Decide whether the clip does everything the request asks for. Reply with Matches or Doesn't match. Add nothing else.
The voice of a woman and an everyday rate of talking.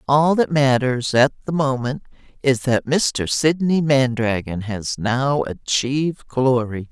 Doesn't match